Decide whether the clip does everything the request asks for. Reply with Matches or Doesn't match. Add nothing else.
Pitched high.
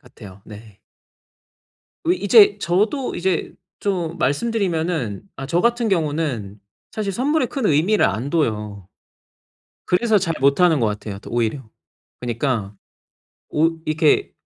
Doesn't match